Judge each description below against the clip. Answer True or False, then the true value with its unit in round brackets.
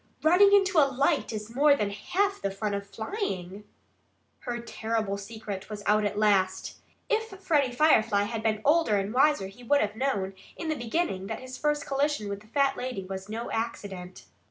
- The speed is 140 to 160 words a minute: False (185 wpm)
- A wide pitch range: True (6.2 semitones)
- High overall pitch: True (225 Hz)